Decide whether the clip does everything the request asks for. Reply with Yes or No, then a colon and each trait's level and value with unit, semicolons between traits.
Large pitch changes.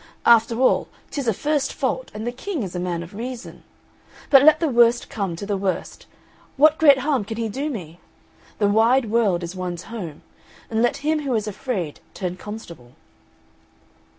Yes: wide, 5.8 semitones